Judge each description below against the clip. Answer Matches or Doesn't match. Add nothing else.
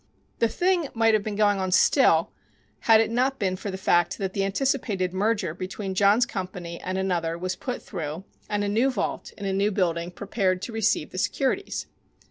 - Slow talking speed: Doesn't match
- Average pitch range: Matches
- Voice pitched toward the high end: Matches